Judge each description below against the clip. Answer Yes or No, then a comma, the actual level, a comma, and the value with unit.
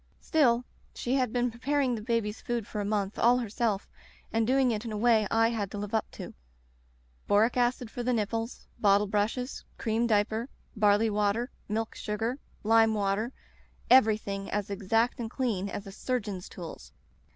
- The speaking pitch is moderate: No, high, 225 Hz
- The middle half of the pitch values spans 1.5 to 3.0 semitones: Yes, narrow, 2.6 semitones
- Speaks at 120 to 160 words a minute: No, average, 175 wpm